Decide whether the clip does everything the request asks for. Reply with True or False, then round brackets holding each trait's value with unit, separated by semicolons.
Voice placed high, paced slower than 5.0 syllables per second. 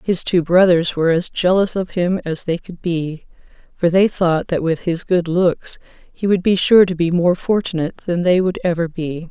False (175 Hz; 4.7 syllables/s)